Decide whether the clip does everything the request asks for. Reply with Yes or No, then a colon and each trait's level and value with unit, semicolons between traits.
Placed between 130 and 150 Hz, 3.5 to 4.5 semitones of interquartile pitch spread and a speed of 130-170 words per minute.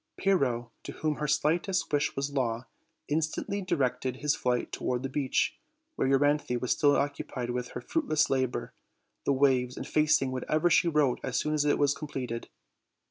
No: medium, 140 Hz; average, 3.1 semitones; average, 165 wpm